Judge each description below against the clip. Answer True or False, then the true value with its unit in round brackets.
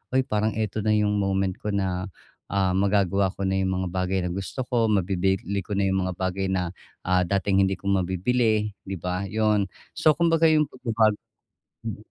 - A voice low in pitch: True (100 Hz)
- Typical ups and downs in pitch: False (2.3 semitones)